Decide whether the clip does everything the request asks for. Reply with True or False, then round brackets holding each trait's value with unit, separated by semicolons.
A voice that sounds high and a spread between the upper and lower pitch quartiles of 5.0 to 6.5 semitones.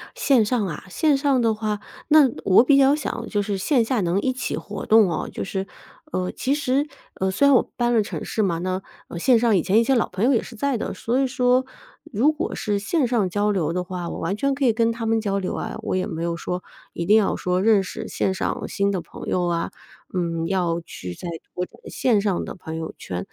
True (210 Hz; 5.3 semitones)